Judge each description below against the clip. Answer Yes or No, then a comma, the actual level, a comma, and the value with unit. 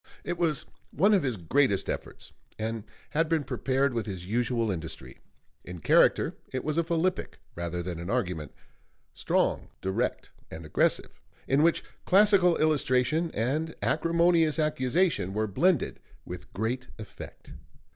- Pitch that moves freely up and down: Yes, wide, 8.7 semitones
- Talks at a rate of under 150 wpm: Yes, slow, 135 wpm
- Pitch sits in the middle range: No, low, 130 Hz